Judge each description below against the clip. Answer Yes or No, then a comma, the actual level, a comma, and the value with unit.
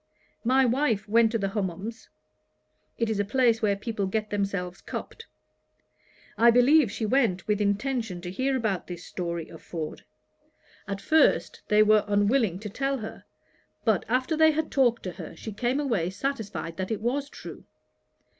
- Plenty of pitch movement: No, average, 4.3 semitones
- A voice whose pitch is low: No, high, 220 Hz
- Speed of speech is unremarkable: Yes, average, 165 wpm